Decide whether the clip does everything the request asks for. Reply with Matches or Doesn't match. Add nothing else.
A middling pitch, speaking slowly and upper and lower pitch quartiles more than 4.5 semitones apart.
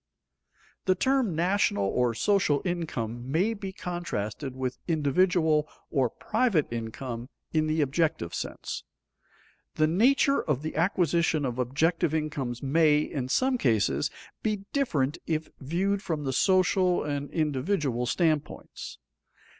Matches